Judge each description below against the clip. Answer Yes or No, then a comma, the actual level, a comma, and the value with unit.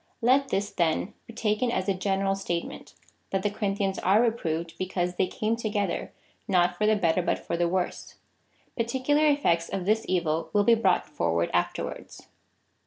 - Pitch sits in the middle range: No, high, 195 Hz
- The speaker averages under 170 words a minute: No, average, 175 wpm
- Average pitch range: Yes, average, 3.8 semitones